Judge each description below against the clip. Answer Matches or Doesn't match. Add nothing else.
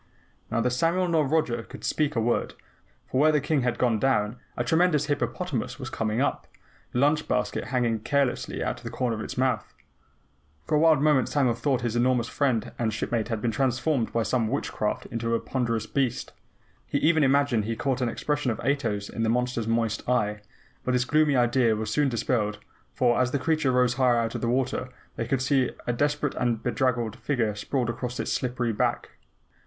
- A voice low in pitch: Matches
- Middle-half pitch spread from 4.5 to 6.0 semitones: Doesn't match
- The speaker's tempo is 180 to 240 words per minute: Matches